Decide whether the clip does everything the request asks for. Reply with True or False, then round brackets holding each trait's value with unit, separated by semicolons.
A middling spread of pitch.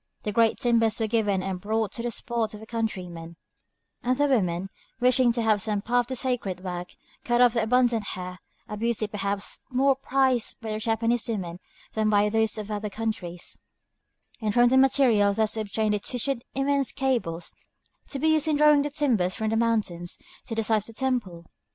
True (3.3 semitones)